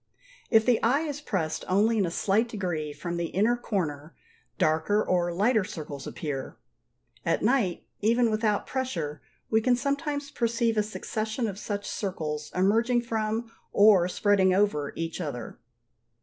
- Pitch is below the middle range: No, high, 205 Hz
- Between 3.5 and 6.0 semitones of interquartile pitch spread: Yes, average, 5.1 semitones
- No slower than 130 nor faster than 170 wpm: Yes, average, 150 wpm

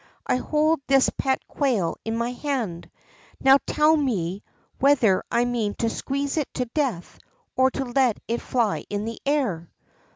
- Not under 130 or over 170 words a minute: Yes, average, 160 wpm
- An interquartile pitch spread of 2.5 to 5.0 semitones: Yes, average, 3.9 semitones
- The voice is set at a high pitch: Yes, very high, 250 Hz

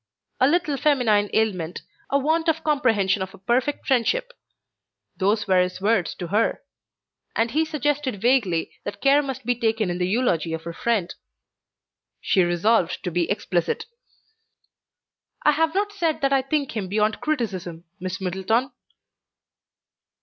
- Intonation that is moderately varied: No, wide, 6.9 semitones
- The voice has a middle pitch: No, high, 225 Hz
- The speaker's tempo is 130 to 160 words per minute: Yes, average, 150 wpm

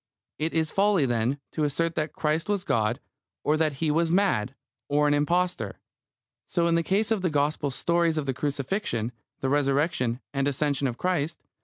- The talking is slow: No, average, 180 wpm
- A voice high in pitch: No, medium, 150 Hz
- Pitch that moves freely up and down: No, average, 3.5 semitones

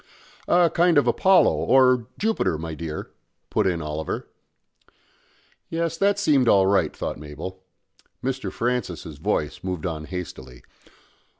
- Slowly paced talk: Yes, slow, 125 wpm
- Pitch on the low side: Yes, very low, 95 Hz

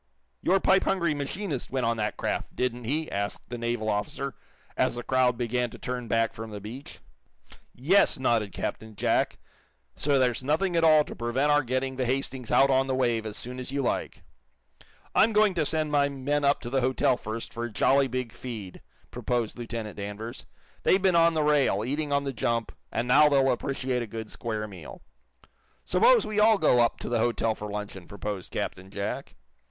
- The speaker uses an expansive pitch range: No, average, 4.0 semitones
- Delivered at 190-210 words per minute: Yes, average, 195 wpm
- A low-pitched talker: Yes, low, 125 Hz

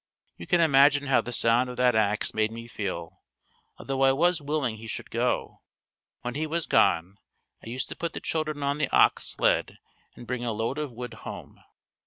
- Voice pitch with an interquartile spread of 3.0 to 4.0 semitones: No, average, 4.4 semitones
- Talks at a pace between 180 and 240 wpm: Yes, average, 200 wpm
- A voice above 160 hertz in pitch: No, low, 125 Hz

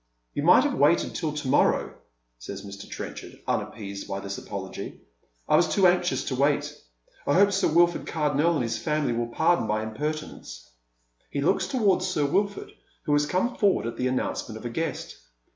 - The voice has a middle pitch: Yes, medium, 145 Hz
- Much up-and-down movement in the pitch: Yes, wide, 7.3 semitones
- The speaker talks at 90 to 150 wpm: No, average, 185 wpm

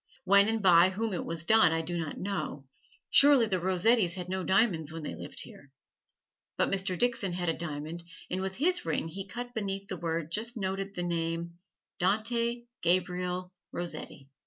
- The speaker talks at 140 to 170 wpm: No, average, 180 wpm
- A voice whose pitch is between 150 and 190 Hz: Yes, medium, 185 Hz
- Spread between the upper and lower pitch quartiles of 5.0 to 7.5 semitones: No, average, 3.7 semitones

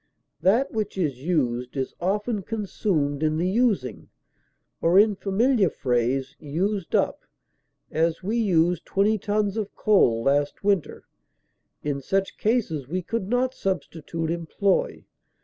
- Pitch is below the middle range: No, medium, 185 Hz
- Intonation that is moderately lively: No, wide, 5.8 semitones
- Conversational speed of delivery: No, slow, 130 wpm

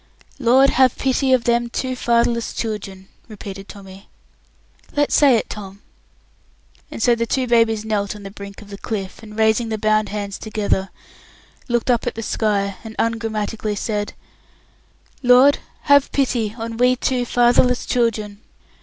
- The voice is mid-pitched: No, high, 225 Hz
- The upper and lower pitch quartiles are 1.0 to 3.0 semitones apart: Yes, average, 2.7 semitones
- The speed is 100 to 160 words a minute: Yes, average, 155 wpm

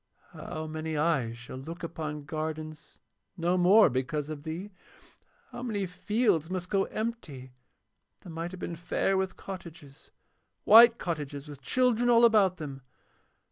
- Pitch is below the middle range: No, medium, 165 Hz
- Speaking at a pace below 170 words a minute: Yes, average, 140 wpm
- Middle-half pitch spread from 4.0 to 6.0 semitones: Yes, average, 4.4 semitones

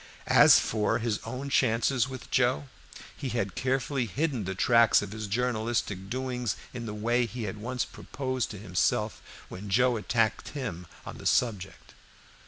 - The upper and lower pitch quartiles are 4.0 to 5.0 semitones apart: No, average, 3.4 semitones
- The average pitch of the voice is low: Yes, low, 115 Hz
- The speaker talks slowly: No, average, 165 wpm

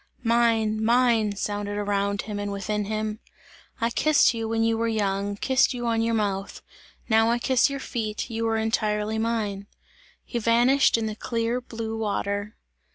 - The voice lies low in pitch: No, high, 220 Hz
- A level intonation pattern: Yes, narrow, 1.9 semitones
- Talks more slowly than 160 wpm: No, average, 165 wpm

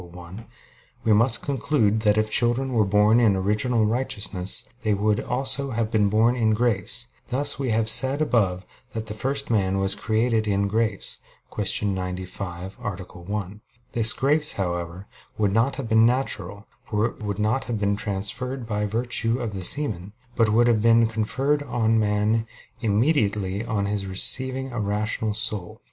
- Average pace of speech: Yes, average, 165 wpm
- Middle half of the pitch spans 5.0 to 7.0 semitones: No, average, 2.9 semitones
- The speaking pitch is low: Yes, low, 110 Hz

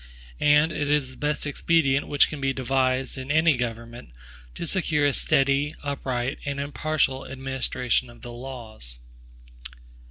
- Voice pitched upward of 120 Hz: Yes, low, 135 Hz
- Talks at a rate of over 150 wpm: No, average, 140 wpm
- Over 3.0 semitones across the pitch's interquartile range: No, narrow, 2.4 semitones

